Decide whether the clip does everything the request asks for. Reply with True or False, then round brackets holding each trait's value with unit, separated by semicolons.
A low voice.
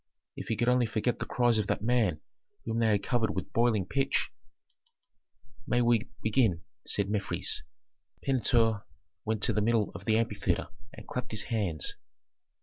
True (110 Hz)